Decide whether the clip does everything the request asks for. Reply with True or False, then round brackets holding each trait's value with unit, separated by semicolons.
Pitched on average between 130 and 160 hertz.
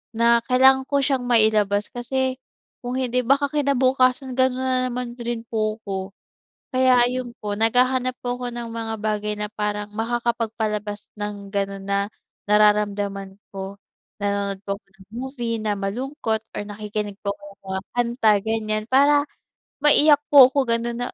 False (230 Hz)